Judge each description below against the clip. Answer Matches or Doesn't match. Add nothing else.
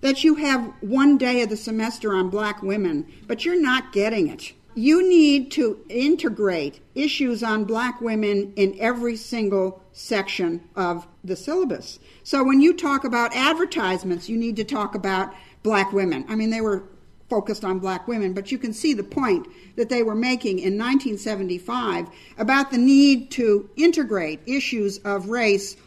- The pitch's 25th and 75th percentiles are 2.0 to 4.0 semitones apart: Doesn't match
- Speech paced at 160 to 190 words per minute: Matches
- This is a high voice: Matches